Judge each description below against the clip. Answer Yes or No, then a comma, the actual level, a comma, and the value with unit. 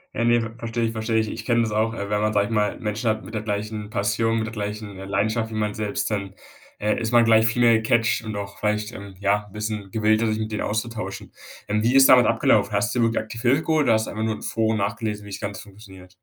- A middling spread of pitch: No, narrow, 1.6 semitones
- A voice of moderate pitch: No, low, 110 Hz